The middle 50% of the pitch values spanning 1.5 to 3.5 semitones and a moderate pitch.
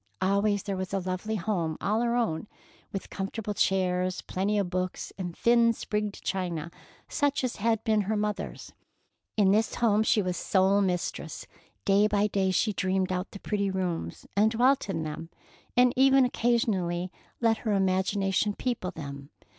No: average, 3.0 semitones; high, 200 Hz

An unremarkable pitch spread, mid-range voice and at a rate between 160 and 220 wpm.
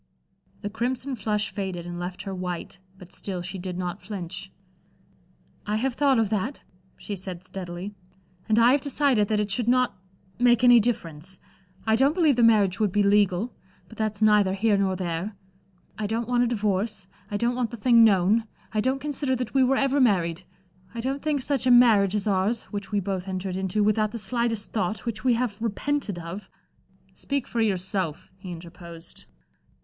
No: average, 4.2 semitones; high, 210 Hz; average, 185 wpm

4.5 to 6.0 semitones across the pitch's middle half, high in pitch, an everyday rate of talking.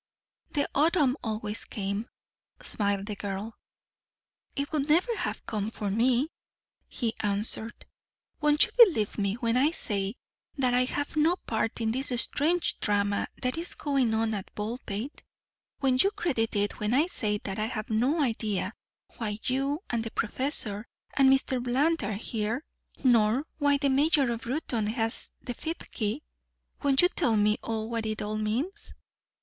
Yes: average, 4.9 semitones; high, 235 Hz; average, 160 wpm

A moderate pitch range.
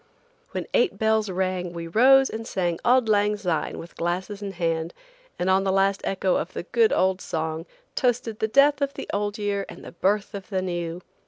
Yes: average, 3.6 semitones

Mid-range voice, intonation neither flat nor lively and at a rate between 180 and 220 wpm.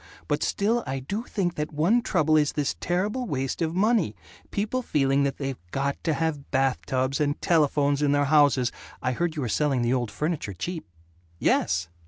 Yes: medium, 145 Hz; average, 4.4 semitones; average, 190 wpm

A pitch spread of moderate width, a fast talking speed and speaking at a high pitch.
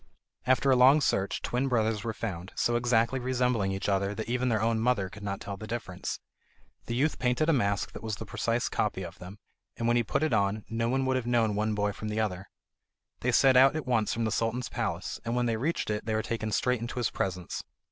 No: average, 3.3 semitones; fast, 245 wpm; low, 115 Hz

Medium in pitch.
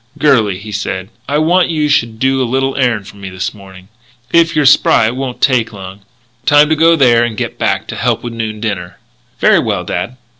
No: low, 120 Hz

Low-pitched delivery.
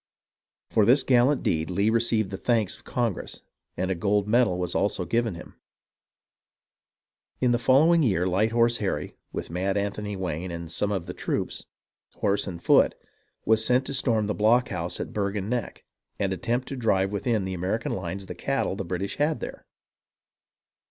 Yes: low, 105 Hz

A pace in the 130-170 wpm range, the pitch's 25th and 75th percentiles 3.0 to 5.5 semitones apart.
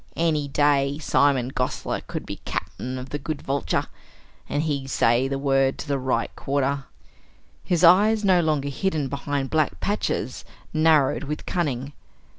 No: average, 150 wpm; narrow, 2.6 semitones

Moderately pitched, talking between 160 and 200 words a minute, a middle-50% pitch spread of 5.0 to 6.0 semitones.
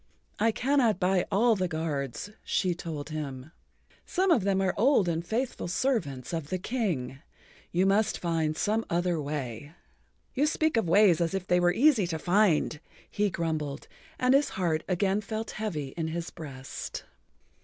Yes: medium, 180 Hz; average, 165 wpm; wide, 5.4 semitones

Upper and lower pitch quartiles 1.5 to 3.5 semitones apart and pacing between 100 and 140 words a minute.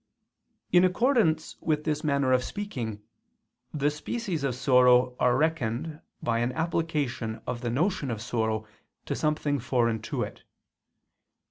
No: average, 4.9 semitones; slow, 135 wpm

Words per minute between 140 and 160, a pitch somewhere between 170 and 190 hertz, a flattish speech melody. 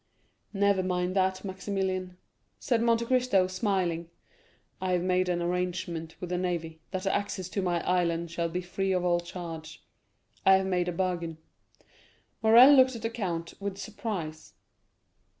Yes: average, 155 wpm; medium, 185 Hz; narrow, 2.2 semitones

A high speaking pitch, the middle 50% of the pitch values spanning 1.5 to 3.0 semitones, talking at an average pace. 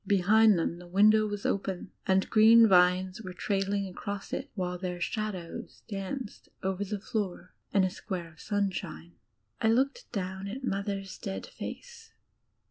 Yes: high, 195 Hz; narrow, 2.6 semitones; average, 150 wpm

